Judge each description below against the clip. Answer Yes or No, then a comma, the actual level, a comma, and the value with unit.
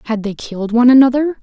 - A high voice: Yes, high, 240 Hz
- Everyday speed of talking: No, fast, 210 wpm